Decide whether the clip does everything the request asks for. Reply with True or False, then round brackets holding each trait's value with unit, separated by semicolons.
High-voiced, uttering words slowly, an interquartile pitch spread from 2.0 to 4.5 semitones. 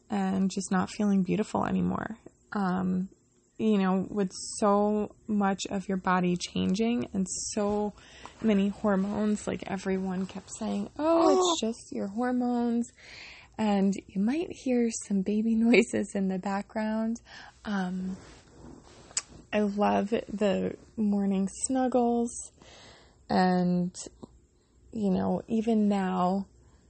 True (205 Hz; 110 wpm; 2.7 semitones)